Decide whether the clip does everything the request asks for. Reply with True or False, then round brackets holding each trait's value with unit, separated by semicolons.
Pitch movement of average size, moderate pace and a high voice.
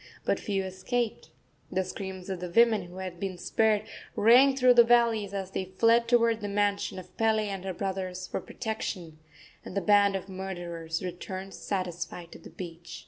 True (3.2 semitones; 180 wpm; 195 Hz)